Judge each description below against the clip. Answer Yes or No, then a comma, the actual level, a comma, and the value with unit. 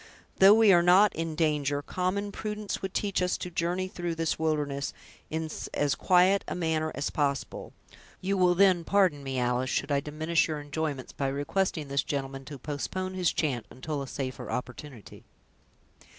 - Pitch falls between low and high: Yes, medium, 160 Hz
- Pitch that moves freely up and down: No, average, 4.5 semitones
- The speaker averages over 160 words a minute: Yes, average, 170 wpm